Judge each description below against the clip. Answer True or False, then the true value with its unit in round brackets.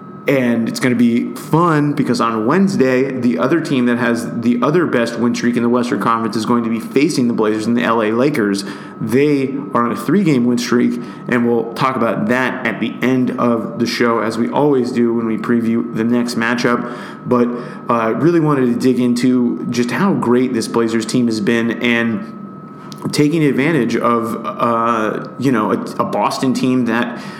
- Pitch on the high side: False (120 Hz)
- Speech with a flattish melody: True (1.8 semitones)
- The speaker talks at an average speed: True (195 wpm)